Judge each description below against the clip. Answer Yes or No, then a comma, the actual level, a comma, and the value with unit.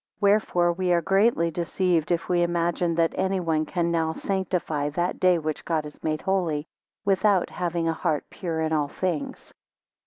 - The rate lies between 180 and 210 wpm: No, average, 165 wpm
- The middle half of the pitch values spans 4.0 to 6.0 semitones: No, narrow, 2.4 semitones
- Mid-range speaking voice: Yes, medium, 170 Hz